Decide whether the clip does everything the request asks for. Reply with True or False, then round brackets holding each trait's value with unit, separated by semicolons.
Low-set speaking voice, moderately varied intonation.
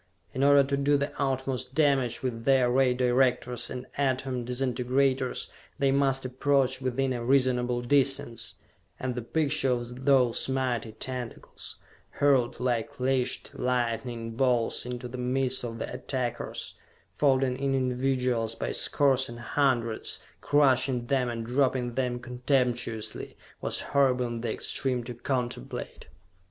False (125 Hz; 1.6 semitones)